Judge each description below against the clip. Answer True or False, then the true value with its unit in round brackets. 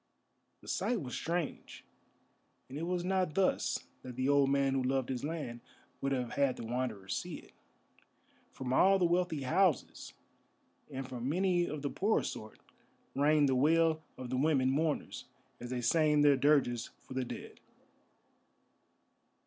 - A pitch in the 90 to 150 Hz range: True (140 Hz)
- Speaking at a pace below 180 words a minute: True (155 wpm)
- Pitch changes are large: False (4.2 semitones)